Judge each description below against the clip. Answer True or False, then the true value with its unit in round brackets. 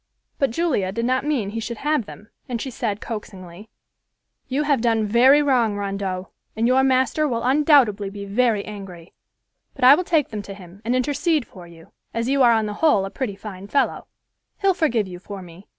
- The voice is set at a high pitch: True (230 Hz)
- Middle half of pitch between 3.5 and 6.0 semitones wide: True (5.0 semitones)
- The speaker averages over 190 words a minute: True (200 wpm)